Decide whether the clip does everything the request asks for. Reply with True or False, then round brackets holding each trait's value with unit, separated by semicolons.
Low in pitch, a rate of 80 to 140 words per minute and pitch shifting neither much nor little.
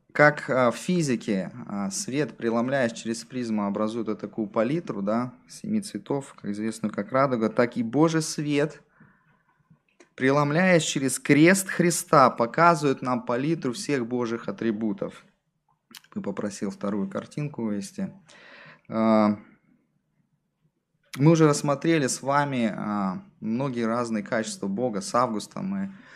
False (130 Hz; 110 wpm; 6.4 semitones)